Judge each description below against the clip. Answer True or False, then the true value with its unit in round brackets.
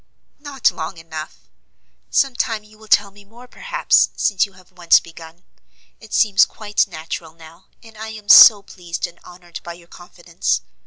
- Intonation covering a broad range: False (4.3 semitones)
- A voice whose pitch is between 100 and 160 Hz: False (190 Hz)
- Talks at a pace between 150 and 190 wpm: True (170 wpm)